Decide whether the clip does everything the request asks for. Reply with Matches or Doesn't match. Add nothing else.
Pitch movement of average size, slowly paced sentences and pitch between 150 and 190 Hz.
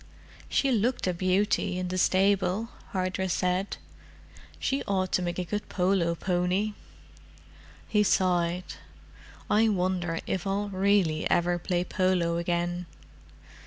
Doesn't match